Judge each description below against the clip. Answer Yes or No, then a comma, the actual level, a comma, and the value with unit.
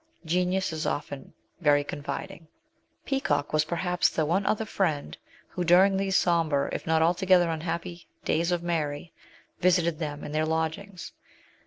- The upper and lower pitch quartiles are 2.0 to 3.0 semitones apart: Yes, narrow, 2.6 semitones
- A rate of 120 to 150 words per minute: Yes, average, 145 wpm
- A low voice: No, medium, 170 Hz